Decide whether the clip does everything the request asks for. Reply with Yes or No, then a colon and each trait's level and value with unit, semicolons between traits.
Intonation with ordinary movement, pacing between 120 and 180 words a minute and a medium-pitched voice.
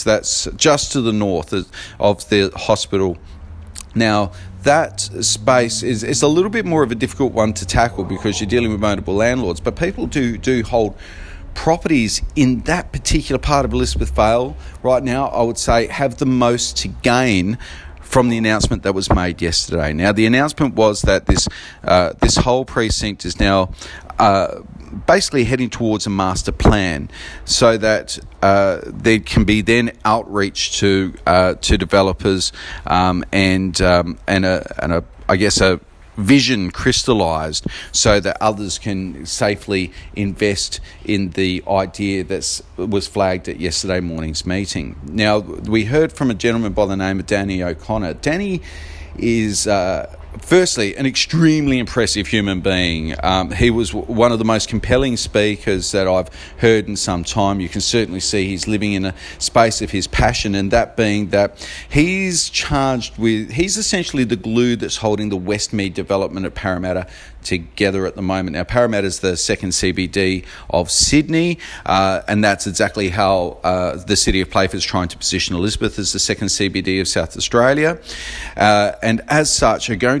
No: average, 4.0 semitones; average, 170 wpm; low, 105 Hz